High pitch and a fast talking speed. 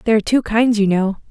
Yes: high, 215 Hz; fast, 275 wpm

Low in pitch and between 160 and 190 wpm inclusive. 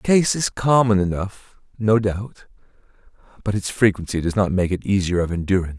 Yes: low, 100 Hz; average, 175 wpm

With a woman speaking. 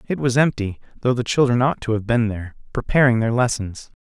No: male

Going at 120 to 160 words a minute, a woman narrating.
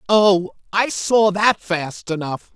Yes: average, 140 wpm; female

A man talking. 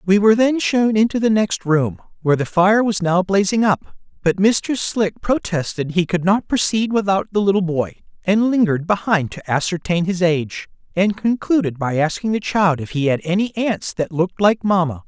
Yes: male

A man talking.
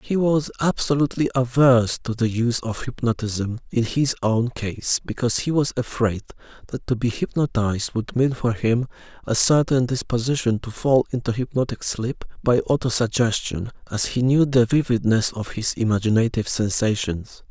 Yes: male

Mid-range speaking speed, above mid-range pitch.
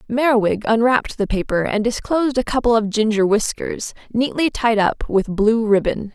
Yes: average, 165 wpm; high, 225 Hz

